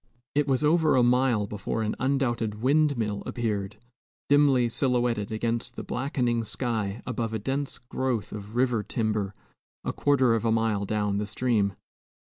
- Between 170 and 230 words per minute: No, average, 150 wpm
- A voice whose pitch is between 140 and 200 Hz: No, low, 115 Hz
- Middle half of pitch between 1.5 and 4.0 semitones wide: Yes, average, 3.7 semitones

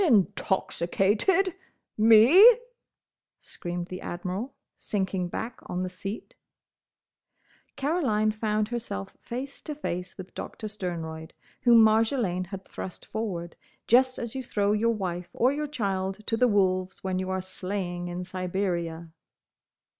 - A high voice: Yes, high, 200 Hz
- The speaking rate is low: Yes, slow, 125 wpm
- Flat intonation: No, average, 4.2 semitones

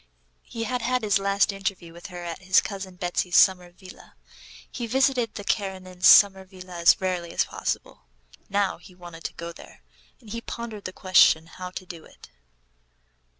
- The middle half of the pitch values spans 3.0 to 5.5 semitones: No, narrow, 2.4 semitones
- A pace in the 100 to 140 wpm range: No, average, 175 wpm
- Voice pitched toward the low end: No, medium, 185 Hz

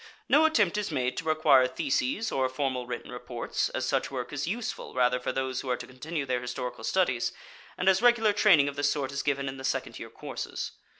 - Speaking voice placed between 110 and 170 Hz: Yes, low, 135 Hz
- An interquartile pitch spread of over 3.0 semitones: Yes, average, 4.7 semitones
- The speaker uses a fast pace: Yes, fast, 220 wpm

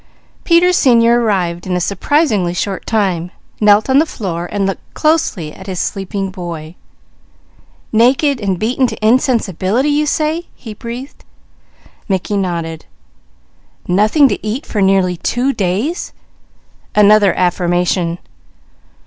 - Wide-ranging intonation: Yes, wide, 5.7 semitones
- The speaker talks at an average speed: No, slow, 115 wpm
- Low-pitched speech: No, high, 205 Hz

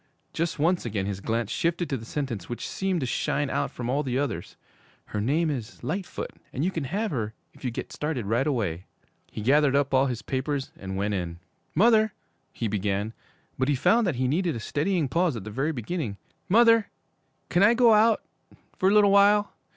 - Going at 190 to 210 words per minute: Yes, fast, 205 wpm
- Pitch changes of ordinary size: No, wide, 7.7 semitones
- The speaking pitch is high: No, medium, 140 Hz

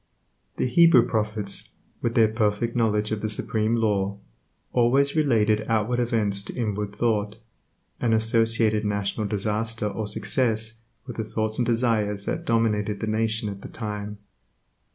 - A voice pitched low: Yes, low, 110 Hz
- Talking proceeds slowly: No, average, 145 wpm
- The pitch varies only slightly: Yes, narrow, 1.8 semitones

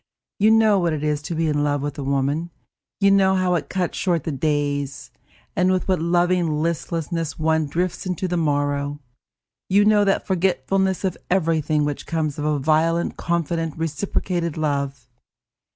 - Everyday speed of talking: Yes, average, 170 wpm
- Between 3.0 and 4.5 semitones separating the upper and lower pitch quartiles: Yes, average, 3.7 semitones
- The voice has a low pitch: No, medium, 165 Hz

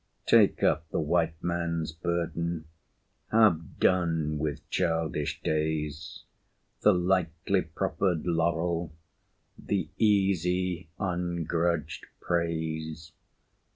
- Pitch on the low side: Yes, very low, 85 Hz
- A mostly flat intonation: Yes, narrow, 1.9 semitones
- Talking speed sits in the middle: No, slow, 85 wpm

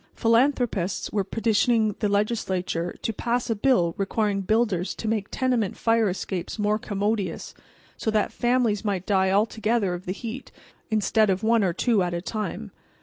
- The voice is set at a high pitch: Yes, high, 210 Hz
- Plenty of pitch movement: No, average, 3.0 semitones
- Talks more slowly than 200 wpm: Yes, average, 165 wpm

